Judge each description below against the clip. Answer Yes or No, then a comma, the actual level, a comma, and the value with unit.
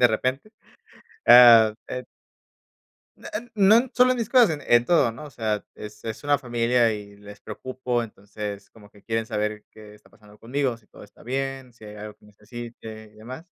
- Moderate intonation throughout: Yes, average, 3.7 semitones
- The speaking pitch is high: No, low, 115 Hz